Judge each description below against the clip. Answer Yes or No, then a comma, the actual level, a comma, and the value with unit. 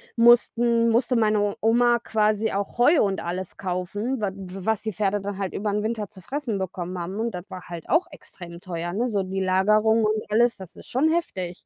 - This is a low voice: No, high, 210 Hz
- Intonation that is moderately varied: Yes, average, 3.6 semitones